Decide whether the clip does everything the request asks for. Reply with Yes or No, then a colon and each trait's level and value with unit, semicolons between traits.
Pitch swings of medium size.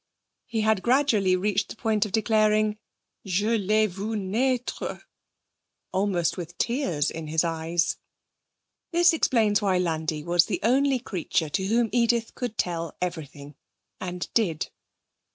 Yes: average, 4.6 semitones